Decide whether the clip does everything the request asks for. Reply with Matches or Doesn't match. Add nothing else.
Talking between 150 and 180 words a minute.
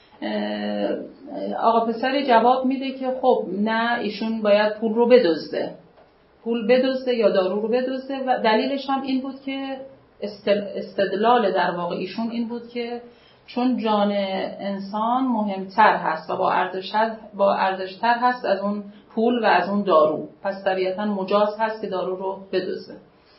Doesn't match